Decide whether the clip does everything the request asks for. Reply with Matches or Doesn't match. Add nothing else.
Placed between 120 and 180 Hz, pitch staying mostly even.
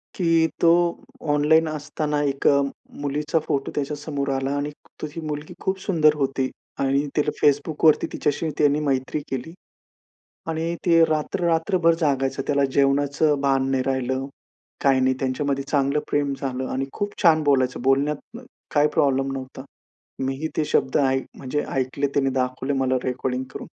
Matches